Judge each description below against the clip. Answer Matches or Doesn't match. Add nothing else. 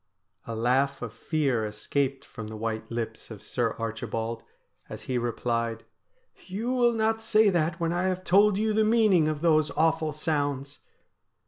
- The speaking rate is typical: Matches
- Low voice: Doesn't match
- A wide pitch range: Matches